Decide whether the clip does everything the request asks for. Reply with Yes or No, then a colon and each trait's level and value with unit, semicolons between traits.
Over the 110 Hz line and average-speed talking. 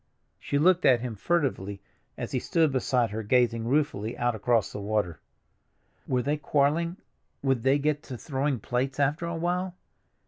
Yes: low, 135 Hz; average, 160 wpm